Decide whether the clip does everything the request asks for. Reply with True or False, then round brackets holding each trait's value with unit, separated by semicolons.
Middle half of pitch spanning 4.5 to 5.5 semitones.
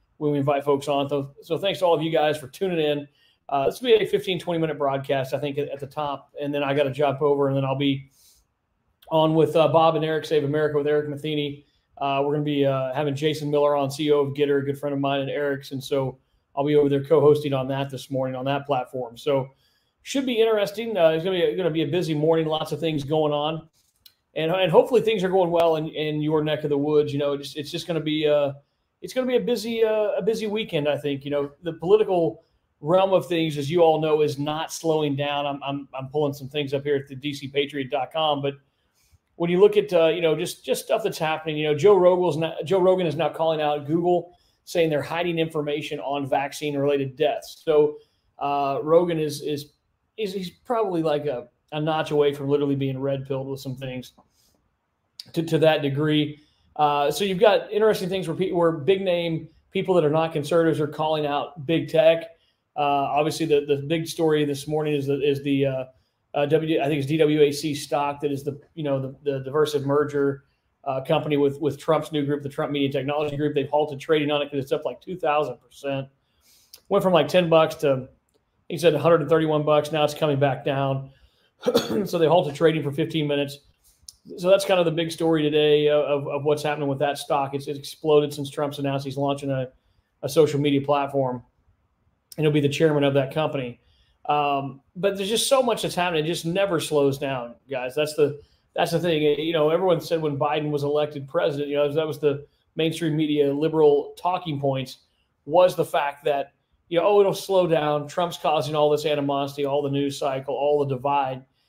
False (2.5 semitones)